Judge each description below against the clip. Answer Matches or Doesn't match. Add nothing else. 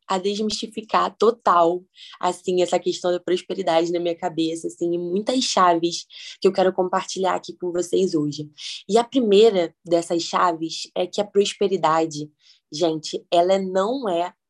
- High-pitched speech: Doesn't match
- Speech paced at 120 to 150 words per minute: Matches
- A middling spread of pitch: Doesn't match